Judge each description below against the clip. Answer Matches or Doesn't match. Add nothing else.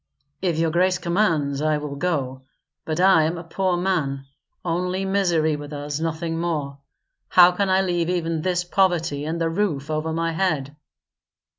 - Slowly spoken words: Doesn't match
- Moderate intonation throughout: Matches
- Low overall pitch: Doesn't match